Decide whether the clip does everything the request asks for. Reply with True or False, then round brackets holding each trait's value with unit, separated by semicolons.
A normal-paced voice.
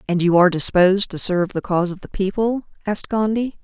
False (215 wpm)